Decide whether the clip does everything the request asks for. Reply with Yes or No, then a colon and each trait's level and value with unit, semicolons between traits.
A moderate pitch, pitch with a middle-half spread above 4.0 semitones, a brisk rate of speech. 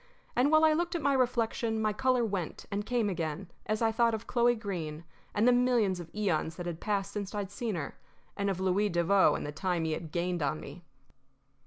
No: high, 205 Hz; average, 5.1 semitones; fast, 220 wpm